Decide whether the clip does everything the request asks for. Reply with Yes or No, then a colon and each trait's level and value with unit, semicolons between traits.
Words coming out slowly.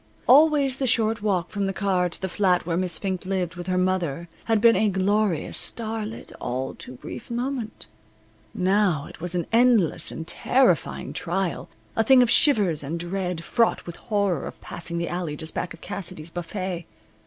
No: average, 185 wpm